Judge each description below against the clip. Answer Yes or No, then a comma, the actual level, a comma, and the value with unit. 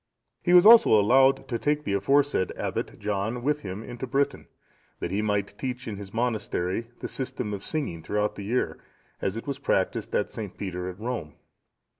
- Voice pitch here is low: Yes, low, 115 Hz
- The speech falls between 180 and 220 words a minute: Yes, average, 185 wpm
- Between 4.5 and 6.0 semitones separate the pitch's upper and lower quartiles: Yes, average, 5.1 semitones